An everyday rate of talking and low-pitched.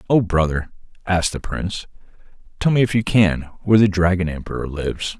Yes: average, 175 wpm; very low, 95 Hz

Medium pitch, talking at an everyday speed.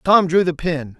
No: medium, 165 Hz; fast, 240 wpm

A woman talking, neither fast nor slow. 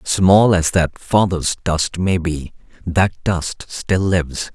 No: male; average, 145 wpm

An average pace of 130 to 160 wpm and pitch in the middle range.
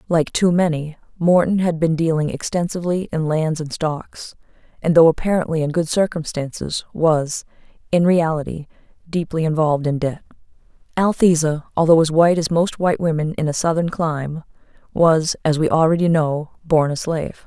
Yes: average, 155 wpm; medium, 160 Hz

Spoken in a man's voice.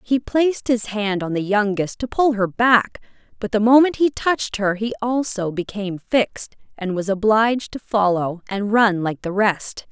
No: female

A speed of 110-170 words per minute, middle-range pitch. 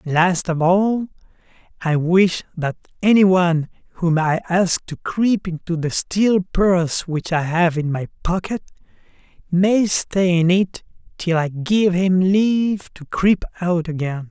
Yes: average, 150 wpm; medium, 180 Hz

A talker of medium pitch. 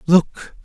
Yes: medium, 170 Hz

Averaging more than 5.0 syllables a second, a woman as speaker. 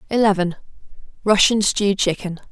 Yes: 5.8 syllables/s; female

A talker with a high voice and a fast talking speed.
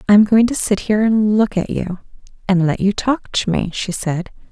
Yes: high, 205 Hz; fast, 240 wpm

